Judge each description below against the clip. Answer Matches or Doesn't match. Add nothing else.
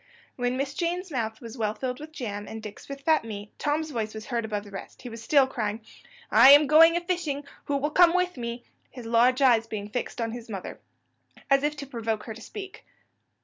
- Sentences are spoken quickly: Matches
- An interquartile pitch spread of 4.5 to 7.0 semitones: Matches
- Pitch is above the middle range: Matches